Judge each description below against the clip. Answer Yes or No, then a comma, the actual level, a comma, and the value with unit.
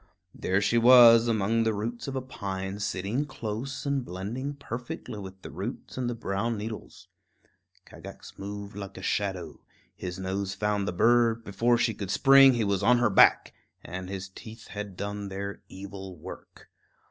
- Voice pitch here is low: Yes, low, 105 Hz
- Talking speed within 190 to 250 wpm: No, average, 170 wpm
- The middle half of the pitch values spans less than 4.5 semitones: Yes, average, 3.3 semitones